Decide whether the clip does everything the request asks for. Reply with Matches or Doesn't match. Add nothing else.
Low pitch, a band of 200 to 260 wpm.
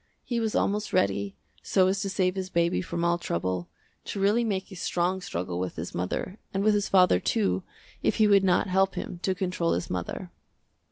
Doesn't match